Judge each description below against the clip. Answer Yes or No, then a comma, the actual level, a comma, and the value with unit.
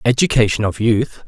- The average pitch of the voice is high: No, low, 115 Hz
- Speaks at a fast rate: No, average, 140 wpm